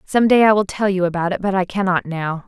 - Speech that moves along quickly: Yes, fast, 290 wpm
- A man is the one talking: No, female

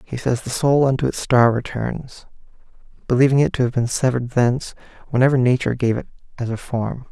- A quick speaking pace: No, average, 185 wpm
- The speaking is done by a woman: No, male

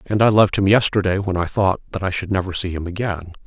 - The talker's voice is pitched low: Yes, very low, 95 Hz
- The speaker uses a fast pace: Yes, fast, 260 wpm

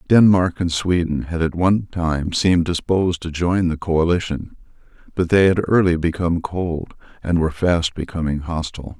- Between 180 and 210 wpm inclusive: No, average, 160 wpm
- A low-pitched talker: Yes, very low, 85 Hz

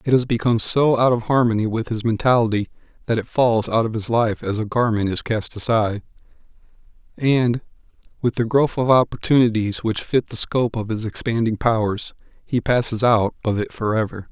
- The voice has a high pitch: No, low, 115 Hz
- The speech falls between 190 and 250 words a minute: No, average, 180 wpm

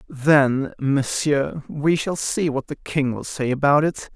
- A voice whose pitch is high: No, medium, 145 Hz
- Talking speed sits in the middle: Yes, average, 175 wpm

